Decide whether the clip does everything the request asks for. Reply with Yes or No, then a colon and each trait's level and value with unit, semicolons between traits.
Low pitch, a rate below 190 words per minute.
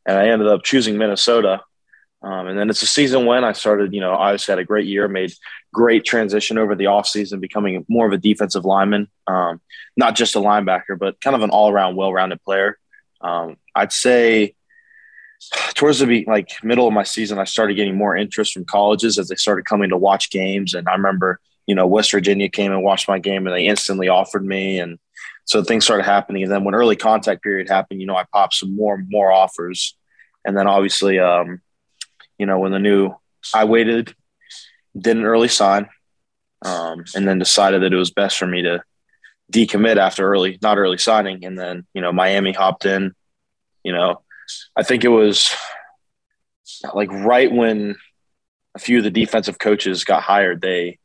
No: low, 100 Hz; average, 195 wpm